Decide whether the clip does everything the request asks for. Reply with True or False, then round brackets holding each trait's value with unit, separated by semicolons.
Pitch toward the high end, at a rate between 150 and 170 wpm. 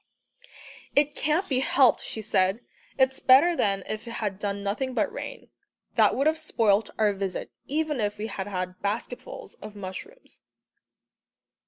True (220 Hz; 155 wpm)